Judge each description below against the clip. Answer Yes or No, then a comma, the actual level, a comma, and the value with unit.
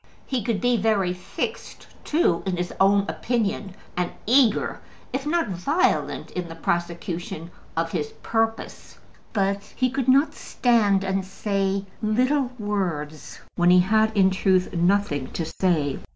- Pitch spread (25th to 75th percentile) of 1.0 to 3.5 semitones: No, average, 4.2 semitones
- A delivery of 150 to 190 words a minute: No, average, 140 wpm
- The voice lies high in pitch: Yes, high, 195 Hz